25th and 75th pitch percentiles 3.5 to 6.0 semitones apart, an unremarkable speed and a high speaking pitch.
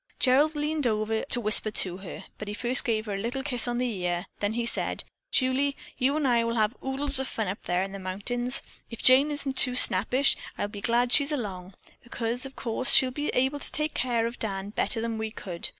No: average, 4.0 semitones; fast, 225 wpm; high, 240 Hz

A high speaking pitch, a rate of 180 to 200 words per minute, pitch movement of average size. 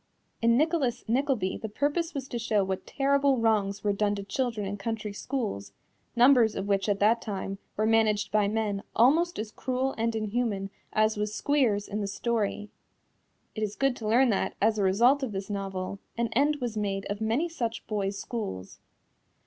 Yes: high, 220 Hz; average, 185 wpm; average, 3.5 semitones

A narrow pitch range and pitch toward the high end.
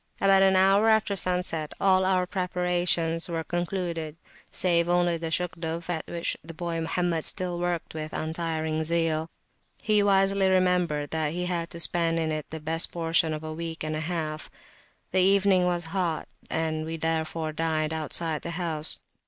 No: narrow, 2.1 semitones; medium, 170 Hz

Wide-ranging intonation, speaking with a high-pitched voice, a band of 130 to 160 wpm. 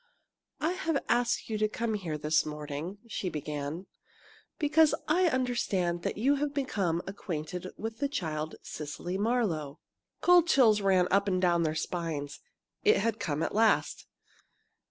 Yes: wide, 7.5 semitones; high, 195 Hz; average, 150 wpm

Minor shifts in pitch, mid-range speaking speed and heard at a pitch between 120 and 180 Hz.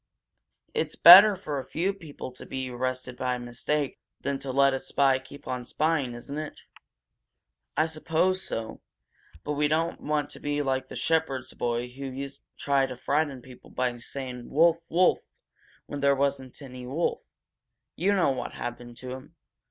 No: average, 3.3 semitones; average, 170 wpm; medium, 140 Hz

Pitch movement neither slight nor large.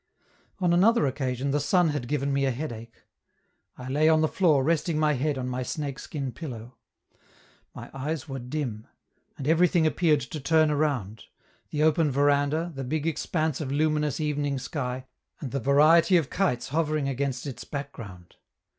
Yes: average, 3.0 semitones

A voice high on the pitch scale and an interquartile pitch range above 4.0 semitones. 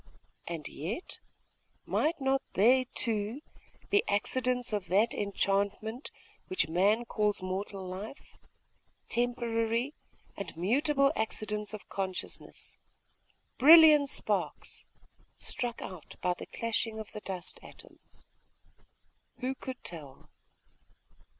Yes: high, 220 Hz; average, 4.5 semitones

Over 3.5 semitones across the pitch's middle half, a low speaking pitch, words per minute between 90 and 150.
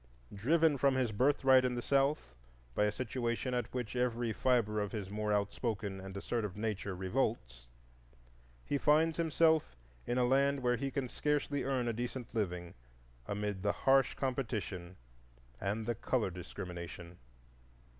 Yes: average, 4.7 semitones; low, 120 Hz; average, 145 wpm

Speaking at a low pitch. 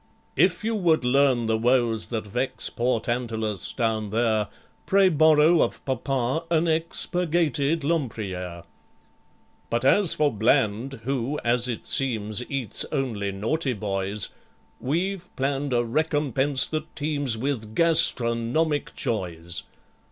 Yes: low, 130 Hz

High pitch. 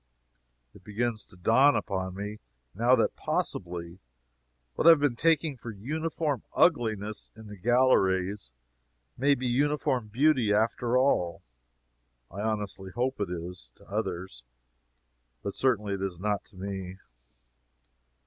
No: low, 105 Hz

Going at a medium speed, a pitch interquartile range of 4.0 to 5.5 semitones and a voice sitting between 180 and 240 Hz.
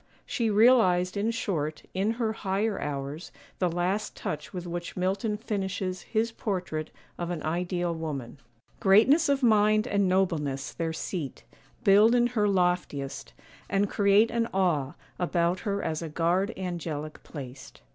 Yes: average, 145 wpm; average, 4.3 semitones; medium, 185 Hz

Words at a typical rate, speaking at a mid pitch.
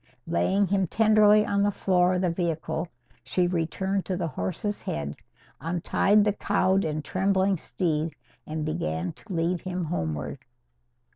Yes: average, 145 wpm; medium, 180 Hz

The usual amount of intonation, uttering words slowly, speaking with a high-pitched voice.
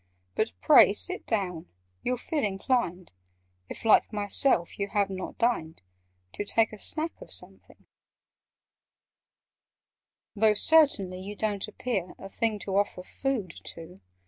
Yes: average, 4.0 semitones; slow, 130 wpm; high, 205 Hz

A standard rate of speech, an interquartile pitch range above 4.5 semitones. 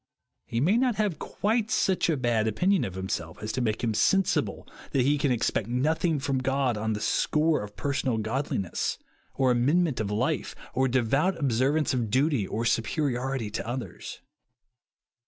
Yes: average, 170 wpm; average, 5.3 semitones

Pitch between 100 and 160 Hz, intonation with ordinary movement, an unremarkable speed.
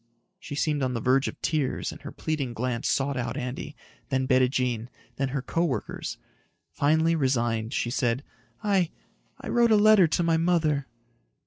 Yes: low, 135 Hz; average, 4.4 semitones; average, 165 wpm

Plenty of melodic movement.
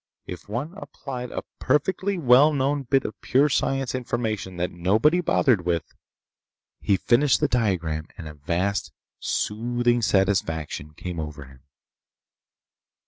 Yes: wide, 7.2 semitones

